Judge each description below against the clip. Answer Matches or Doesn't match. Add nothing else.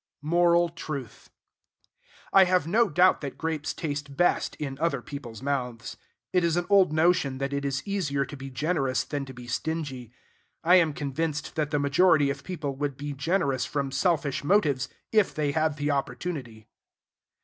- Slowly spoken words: Doesn't match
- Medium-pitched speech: Matches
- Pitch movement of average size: Matches